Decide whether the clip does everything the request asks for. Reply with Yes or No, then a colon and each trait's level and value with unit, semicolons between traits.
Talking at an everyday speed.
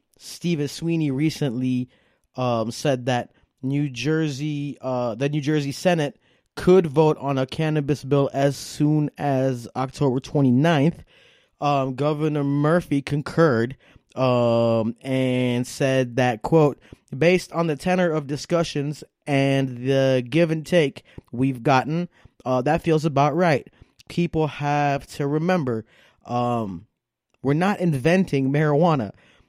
No: slow, 120 wpm